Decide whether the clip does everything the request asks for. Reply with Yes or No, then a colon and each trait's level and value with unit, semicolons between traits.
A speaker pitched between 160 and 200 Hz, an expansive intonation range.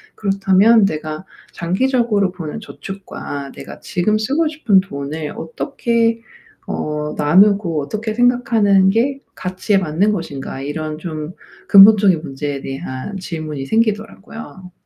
Yes: high, 190 Hz; wide, 5.8 semitones